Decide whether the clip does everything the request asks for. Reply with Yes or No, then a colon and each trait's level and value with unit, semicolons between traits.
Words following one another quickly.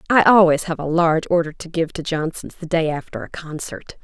Yes: fast, 225 wpm